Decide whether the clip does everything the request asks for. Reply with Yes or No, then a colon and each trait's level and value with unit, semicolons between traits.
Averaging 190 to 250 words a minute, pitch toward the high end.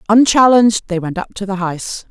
Yes: average, 200 wpm; high, 205 Hz